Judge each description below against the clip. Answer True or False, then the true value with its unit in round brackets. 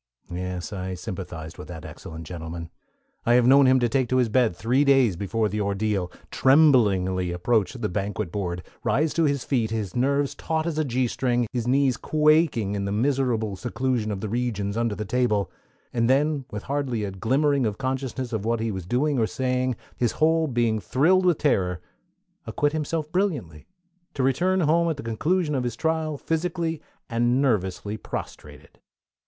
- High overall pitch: False (120 Hz)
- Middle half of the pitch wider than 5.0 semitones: True (5.5 semitones)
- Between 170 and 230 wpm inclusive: True (180 wpm)